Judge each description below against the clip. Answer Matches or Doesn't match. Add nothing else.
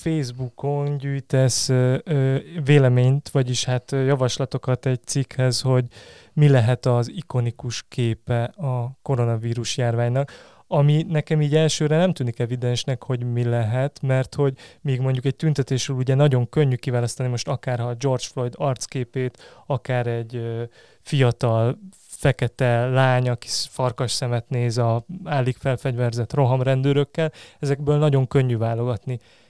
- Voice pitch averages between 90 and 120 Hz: Doesn't match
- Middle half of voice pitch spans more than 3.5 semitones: Doesn't match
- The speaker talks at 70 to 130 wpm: Matches